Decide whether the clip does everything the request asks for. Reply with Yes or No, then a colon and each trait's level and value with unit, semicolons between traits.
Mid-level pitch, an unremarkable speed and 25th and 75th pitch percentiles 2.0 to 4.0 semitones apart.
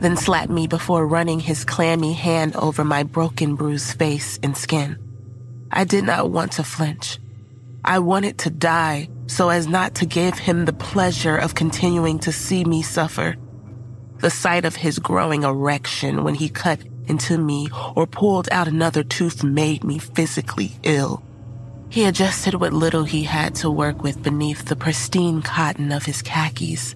Yes: medium, 155 Hz; average, 165 wpm; average, 3.2 semitones